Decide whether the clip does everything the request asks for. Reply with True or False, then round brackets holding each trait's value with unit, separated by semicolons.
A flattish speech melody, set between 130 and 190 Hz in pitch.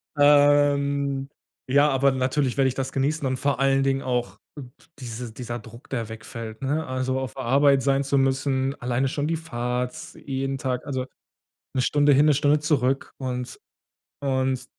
True (1.9 semitones; 135 Hz)